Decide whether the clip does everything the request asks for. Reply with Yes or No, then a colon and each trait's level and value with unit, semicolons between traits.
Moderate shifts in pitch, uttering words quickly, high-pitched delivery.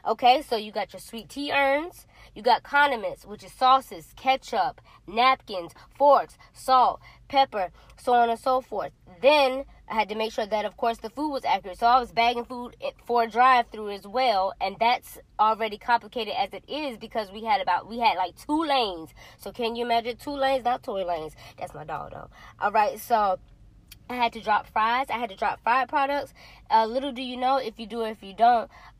Yes: average, 3.8 semitones; fast, 215 wpm; high, 235 Hz